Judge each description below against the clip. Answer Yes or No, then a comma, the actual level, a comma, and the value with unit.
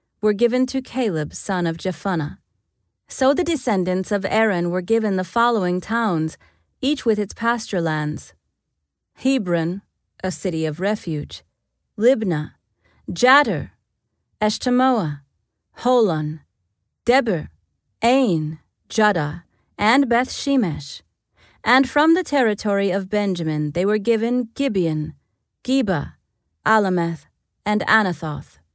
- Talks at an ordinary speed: No, slow, 105 wpm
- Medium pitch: No, high, 200 Hz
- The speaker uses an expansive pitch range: Yes, wide, 6.9 semitones